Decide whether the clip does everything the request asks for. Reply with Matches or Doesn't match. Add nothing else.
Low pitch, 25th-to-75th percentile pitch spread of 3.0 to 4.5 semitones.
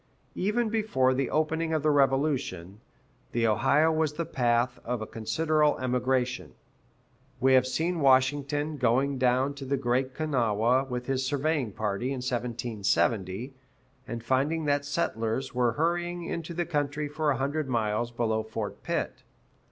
Matches